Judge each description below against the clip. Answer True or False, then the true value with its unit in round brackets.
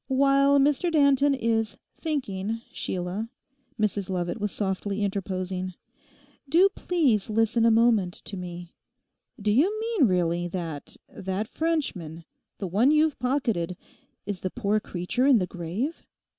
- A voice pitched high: True (215 Hz)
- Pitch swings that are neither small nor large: False (6.8 semitones)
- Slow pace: True (125 wpm)